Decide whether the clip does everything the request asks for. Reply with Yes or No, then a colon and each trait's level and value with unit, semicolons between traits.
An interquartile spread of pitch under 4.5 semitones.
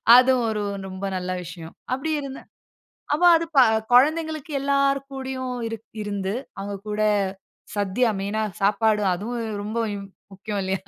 No: average, 5.2 semitones